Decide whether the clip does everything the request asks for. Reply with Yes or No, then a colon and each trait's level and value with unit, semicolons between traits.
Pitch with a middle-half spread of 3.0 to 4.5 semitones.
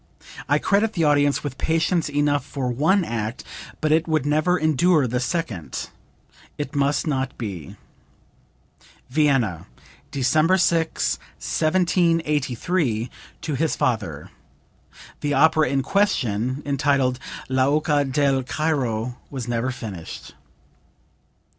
Yes: average, 4.0 semitones